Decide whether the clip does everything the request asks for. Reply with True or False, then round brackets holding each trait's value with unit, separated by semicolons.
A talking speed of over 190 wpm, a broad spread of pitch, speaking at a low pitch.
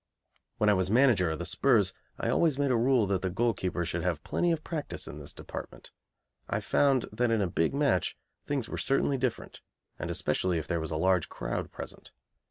True (205 wpm; 6.9 semitones; 105 Hz)